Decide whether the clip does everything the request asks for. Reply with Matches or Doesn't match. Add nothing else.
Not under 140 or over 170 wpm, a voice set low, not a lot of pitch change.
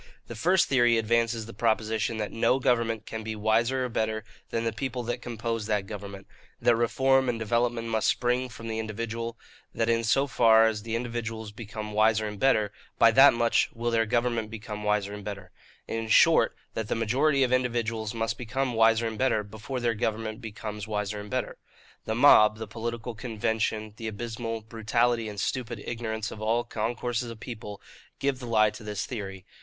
Doesn't match